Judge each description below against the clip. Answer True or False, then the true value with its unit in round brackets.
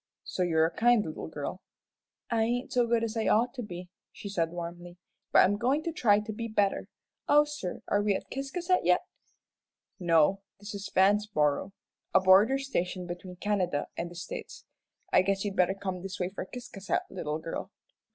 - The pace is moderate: True (185 wpm)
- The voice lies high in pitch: True (195 Hz)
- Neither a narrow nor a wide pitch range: True (4.4 semitones)